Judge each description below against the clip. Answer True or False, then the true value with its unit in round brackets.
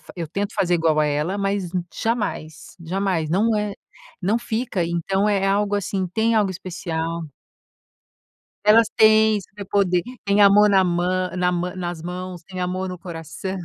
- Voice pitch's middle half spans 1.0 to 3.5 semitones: True (2.7 semitones)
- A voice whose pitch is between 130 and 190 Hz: True (185 Hz)